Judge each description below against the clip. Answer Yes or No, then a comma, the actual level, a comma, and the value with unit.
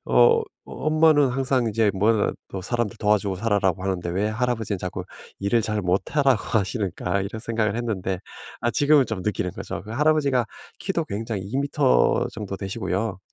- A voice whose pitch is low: Yes, low, 110 Hz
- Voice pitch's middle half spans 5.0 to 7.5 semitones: No, average, 4.2 semitones